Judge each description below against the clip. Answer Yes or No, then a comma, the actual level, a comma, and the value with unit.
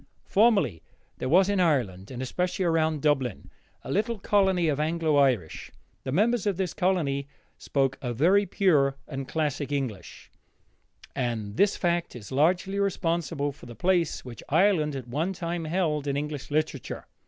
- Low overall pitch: No, medium, 155 Hz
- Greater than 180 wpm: No, average, 155 wpm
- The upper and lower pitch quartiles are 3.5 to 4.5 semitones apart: No, average, 5.1 semitones